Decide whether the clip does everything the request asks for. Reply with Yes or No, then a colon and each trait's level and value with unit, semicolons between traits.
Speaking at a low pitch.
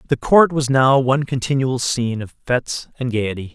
Yes: low, 130 Hz